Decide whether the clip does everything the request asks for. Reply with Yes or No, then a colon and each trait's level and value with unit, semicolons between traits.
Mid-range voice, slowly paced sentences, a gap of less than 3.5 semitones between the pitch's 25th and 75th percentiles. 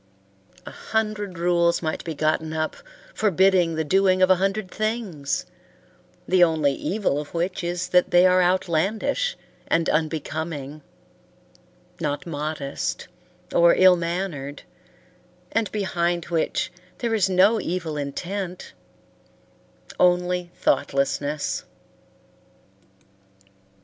Yes: medium, 175 Hz; slow, 105 wpm; average, 3.1 semitones